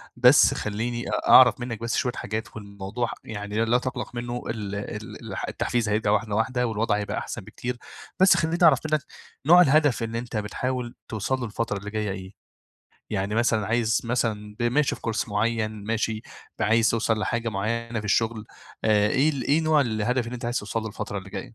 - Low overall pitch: Yes, low, 115 Hz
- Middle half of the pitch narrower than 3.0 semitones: Yes, narrow, 2.5 semitones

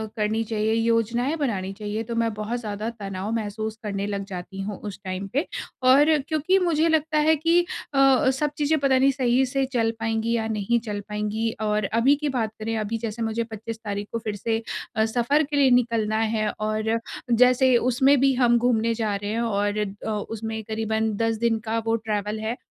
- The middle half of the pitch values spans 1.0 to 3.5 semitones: Yes, average, 2.8 semitones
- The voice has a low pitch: No, high, 225 Hz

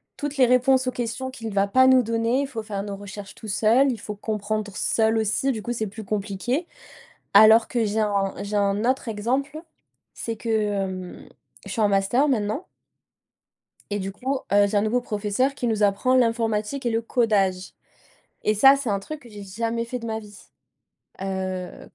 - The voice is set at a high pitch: Yes, high, 220 Hz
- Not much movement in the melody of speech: No, average, 3.5 semitones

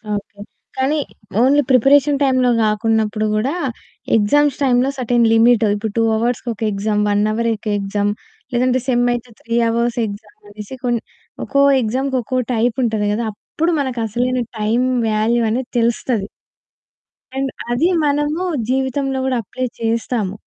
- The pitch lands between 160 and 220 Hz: No, high, 240 Hz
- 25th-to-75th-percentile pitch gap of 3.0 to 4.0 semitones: Yes, average, 3.3 semitones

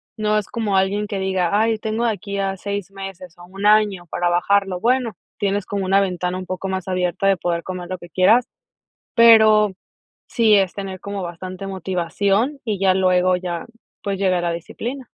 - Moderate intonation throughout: No, narrow, 2.3 semitones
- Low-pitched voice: No, high, 195 Hz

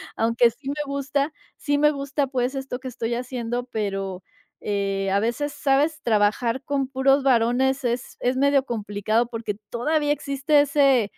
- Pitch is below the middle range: No, very high, 255 Hz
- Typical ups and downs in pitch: Yes, average, 3.5 semitones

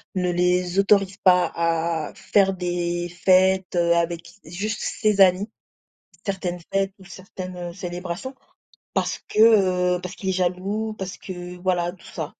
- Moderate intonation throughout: No, narrow, 1.7 semitones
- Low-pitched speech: No, medium, 180 Hz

